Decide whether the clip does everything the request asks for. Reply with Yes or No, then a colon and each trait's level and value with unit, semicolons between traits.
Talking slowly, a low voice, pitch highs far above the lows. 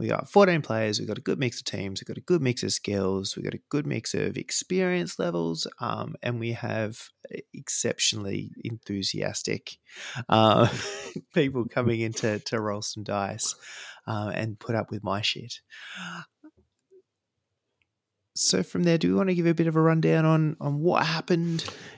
No: average, 175 wpm; low, 115 Hz; wide, 7.4 semitones